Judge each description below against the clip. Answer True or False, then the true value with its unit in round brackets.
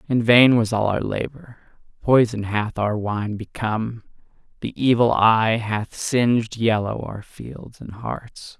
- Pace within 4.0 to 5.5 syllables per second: False (3.8 syllables/s)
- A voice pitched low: True (110 Hz)